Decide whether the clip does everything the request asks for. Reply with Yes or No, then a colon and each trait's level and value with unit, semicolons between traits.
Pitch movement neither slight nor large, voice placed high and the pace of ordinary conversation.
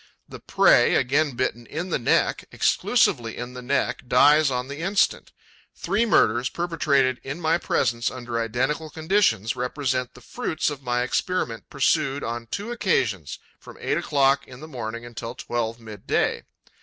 No: average, 4.5 semitones; low, 130 Hz; average, 155 wpm